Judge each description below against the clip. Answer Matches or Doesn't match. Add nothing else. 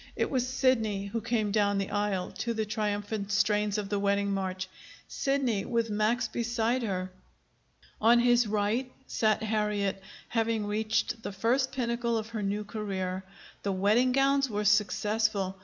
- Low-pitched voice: Doesn't match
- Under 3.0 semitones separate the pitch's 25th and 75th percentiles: Matches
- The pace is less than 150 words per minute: Doesn't match